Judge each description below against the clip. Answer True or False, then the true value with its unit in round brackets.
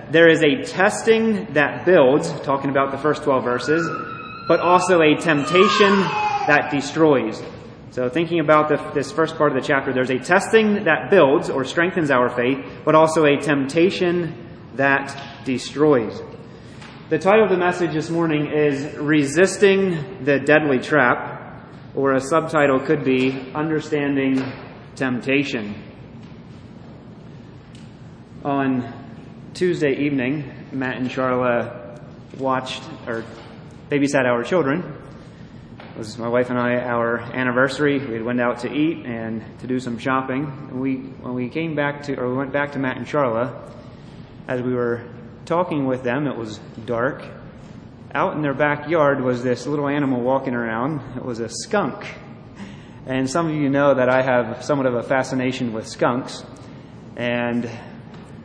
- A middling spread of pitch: True (3.4 semitones)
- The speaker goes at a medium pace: True (150 wpm)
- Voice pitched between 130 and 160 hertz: True (135 Hz)